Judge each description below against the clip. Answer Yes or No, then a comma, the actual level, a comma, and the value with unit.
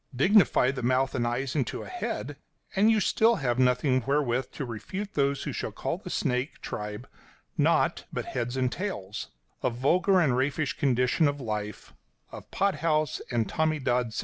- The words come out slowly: No, average, 175 wpm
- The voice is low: Yes, low, 130 Hz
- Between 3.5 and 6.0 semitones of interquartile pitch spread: Yes, average, 4.2 semitones